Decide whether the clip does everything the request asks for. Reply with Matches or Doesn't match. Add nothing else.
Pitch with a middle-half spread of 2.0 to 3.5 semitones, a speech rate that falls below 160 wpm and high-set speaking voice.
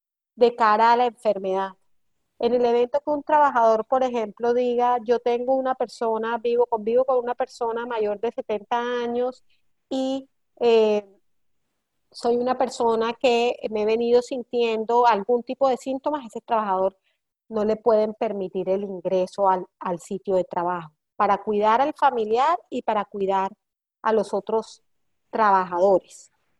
Matches